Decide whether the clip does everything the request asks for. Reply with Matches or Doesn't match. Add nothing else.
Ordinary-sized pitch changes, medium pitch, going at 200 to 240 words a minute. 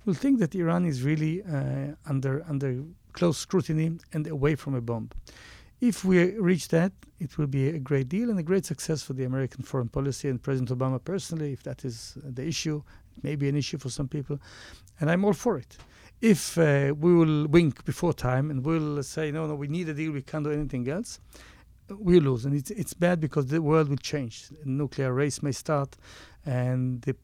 Matches